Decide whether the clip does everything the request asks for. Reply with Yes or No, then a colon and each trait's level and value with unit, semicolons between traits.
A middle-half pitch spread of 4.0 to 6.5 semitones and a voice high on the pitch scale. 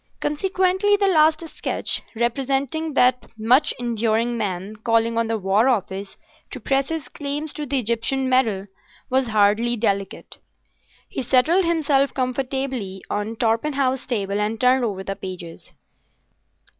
Yes: average, 4.4 semitones; high, 245 Hz